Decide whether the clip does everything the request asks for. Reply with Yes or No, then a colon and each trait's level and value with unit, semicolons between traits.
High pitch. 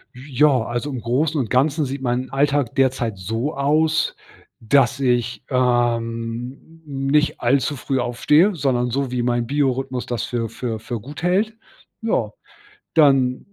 No: low, 130 Hz